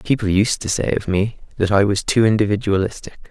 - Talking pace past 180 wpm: Yes, average, 200 wpm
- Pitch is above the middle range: No, low, 105 Hz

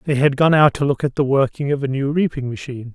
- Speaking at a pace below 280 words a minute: No, fast, 285 wpm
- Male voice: Yes, male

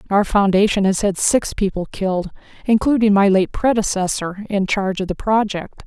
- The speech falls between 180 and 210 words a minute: No, average, 155 wpm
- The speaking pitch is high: Yes, high, 200 Hz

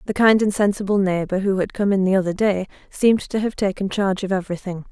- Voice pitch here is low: No, high, 195 Hz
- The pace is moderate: No, fast, 230 wpm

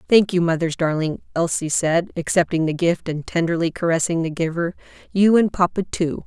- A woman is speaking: Yes, female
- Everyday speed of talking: Yes, average, 170 wpm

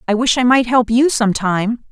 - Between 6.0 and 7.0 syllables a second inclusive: No, 4.7 syllables/s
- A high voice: Yes, high, 230 Hz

